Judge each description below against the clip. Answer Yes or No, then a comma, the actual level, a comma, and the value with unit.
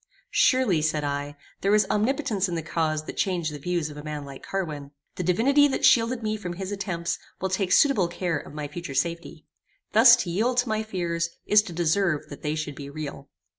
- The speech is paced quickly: Yes, fast, 210 wpm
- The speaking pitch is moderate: Yes, medium, 175 Hz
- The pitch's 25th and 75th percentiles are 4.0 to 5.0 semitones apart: No, wide, 5.4 semitones